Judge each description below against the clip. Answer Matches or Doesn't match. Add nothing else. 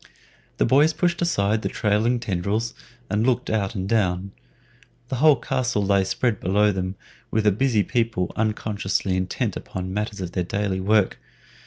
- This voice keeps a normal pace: Matches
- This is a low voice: Matches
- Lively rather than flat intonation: Doesn't match